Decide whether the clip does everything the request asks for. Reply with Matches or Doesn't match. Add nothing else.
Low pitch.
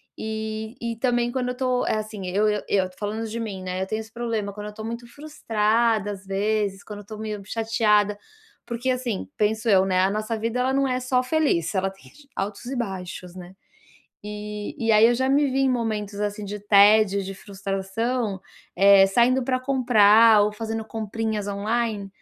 Doesn't match